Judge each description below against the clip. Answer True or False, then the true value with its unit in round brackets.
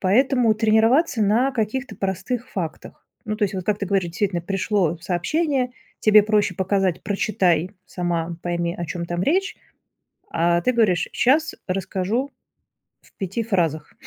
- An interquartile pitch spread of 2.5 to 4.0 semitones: False (4.7 semitones)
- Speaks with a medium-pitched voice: False (200 Hz)